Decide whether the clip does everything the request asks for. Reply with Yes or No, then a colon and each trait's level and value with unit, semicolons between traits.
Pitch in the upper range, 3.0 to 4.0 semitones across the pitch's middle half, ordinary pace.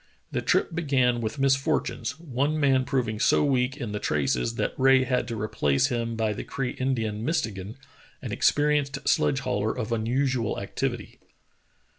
No: low, 125 Hz; average, 3.7 semitones; average, 155 wpm